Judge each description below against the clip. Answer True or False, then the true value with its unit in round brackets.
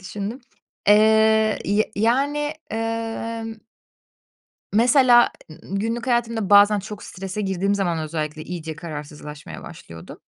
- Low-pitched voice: False (210 Hz)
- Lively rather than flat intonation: False (4.4 semitones)